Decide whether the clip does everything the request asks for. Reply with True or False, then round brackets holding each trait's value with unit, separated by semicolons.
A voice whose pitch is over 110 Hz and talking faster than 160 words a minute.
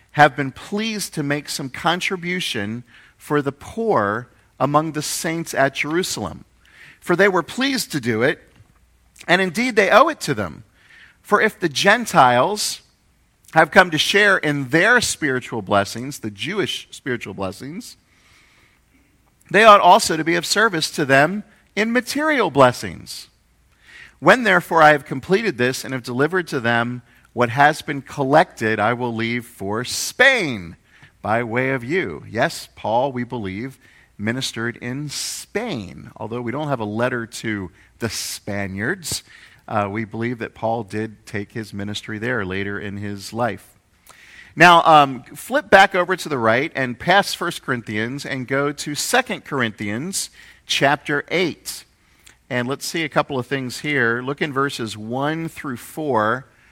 False (135 Hz; 150 wpm)